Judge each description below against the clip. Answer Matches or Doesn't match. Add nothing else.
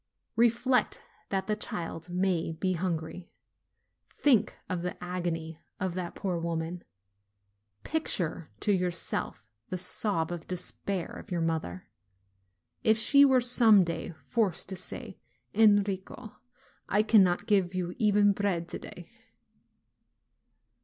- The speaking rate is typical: Doesn't match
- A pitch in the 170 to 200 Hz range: Matches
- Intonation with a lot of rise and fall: Doesn't match